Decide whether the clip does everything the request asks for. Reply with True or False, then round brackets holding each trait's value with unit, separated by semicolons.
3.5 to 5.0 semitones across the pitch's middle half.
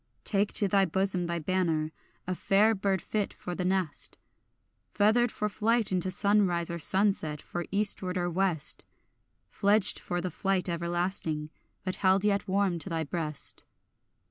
False (2.7 semitones)